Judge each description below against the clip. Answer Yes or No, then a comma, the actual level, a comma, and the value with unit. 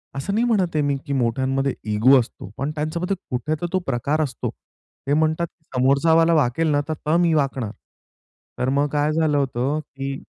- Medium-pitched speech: Yes, medium, 145 Hz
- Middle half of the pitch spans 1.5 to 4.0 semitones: Yes, average, 2.8 semitones